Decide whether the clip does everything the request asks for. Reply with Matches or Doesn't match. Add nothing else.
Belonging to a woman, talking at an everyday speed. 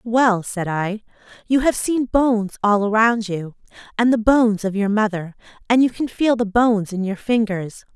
Matches